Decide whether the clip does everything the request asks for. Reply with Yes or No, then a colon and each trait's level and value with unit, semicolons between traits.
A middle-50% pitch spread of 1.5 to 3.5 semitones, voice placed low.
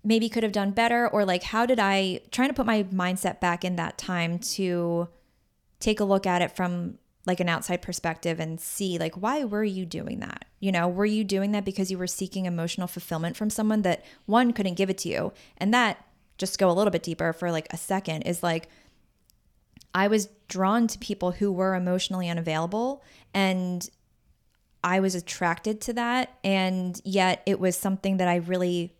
No: average, 3.1 semitones; high, 190 Hz